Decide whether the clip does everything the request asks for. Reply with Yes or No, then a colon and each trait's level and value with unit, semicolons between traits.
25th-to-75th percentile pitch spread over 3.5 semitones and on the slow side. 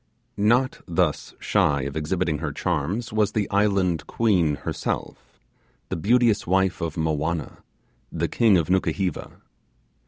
Yes: average, 4.5 semitones; slow, 125 wpm